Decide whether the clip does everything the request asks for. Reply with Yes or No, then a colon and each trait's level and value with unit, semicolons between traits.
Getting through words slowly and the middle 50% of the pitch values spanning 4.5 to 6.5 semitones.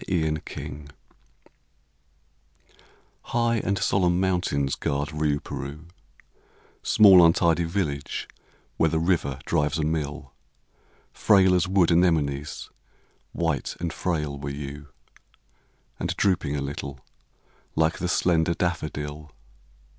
No: slow, 100 wpm; average, 3.3 semitones